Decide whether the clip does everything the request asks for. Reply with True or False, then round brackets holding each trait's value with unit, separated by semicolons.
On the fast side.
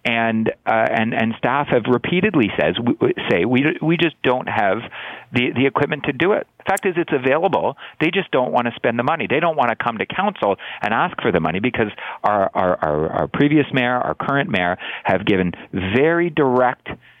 True (210 wpm)